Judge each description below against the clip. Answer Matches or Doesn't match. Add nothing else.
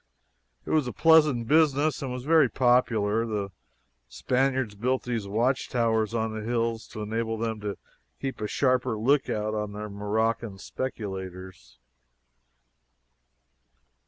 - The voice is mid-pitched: Doesn't match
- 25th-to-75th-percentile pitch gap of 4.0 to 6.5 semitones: Doesn't match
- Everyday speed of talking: Doesn't match